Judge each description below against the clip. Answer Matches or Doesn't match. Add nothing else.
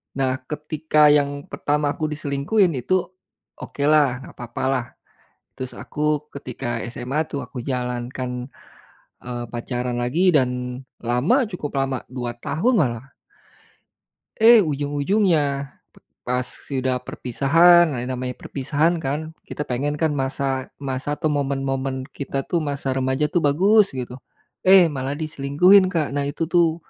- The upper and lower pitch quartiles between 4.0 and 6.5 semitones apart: Doesn't match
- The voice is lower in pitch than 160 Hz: Matches